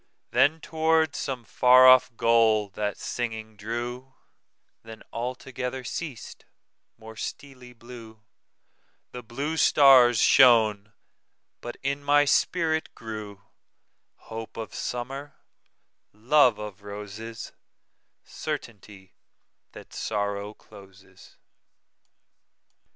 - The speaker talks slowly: Yes, slow, 80 wpm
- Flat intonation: No, average, 3.6 semitones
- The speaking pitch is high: No, low, 120 Hz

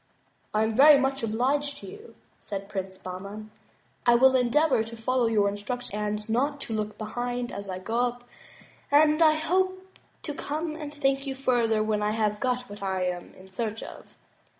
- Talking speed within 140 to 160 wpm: No, average, 185 wpm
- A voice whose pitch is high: Yes, high, 240 Hz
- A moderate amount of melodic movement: Yes, average, 4.6 semitones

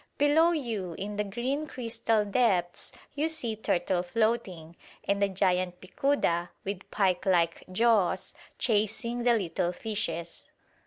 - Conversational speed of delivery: No, slow, 125 wpm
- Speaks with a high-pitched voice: Yes, high, 205 Hz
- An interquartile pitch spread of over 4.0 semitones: Yes, average, 4.7 semitones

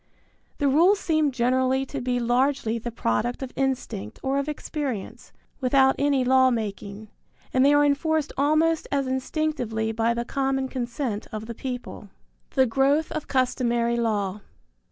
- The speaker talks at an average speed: Yes, average, 155 wpm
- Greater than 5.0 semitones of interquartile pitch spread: No, average, 3.2 semitones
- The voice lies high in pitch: Yes, very high, 260 Hz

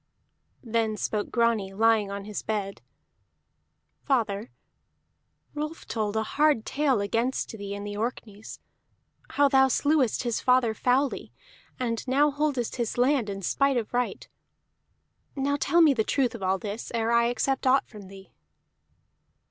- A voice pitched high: Yes, high, 235 Hz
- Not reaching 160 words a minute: Yes, average, 145 wpm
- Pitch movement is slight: No, average, 4.2 semitones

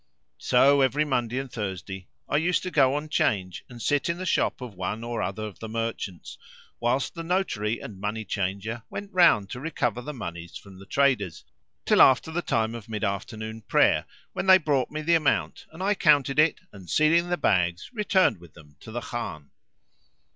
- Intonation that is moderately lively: No, wide, 7.1 semitones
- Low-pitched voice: Yes, low, 120 Hz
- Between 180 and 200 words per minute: Yes, average, 195 wpm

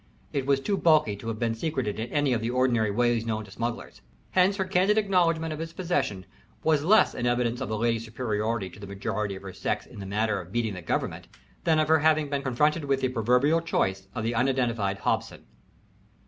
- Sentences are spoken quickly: Yes, fast, 220 wpm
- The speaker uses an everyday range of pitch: No, wide, 6.0 semitones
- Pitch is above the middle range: No, low, 120 Hz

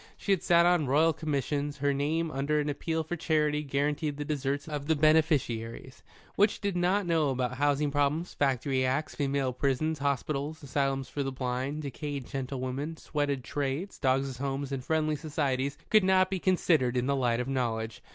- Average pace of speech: Yes, average, 180 wpm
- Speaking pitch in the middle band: Yes, medium, 145 Hz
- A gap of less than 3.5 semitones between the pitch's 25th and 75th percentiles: Yes, average, 2.7 semitones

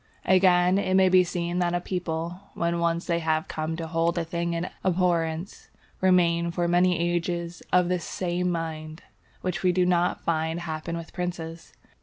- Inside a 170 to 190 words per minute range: Yes, average, 175 wpm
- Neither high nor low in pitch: Yes, medium, 170 Hz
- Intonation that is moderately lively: No, narrow, 1.3 semitones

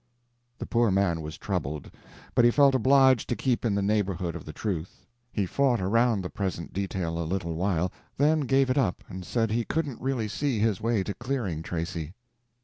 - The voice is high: No, low, 105 Hz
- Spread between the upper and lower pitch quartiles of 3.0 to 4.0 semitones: No, wide, 5.5 semitones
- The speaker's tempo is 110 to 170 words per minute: No, average, 195 wpm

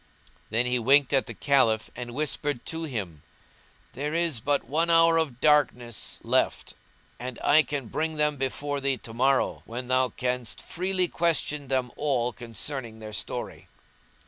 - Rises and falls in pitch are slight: No, average, 3.7 semitones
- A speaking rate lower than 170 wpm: Yes, average, 155 wpm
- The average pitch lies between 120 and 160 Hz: Yes, low, 135 Hz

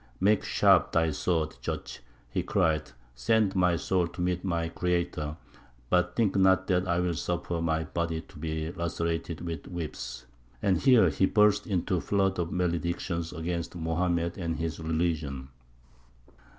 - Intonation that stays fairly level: Yes, narrow, 1.9 semitones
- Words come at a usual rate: Yes, average, 150 wpm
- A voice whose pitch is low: Yes, very low, 85 Hz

